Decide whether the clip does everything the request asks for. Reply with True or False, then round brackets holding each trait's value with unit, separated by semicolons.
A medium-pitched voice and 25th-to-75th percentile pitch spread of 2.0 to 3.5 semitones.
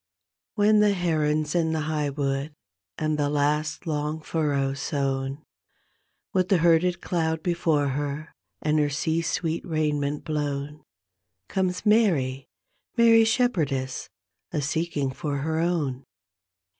True (155 Hz; 2.9 semitones)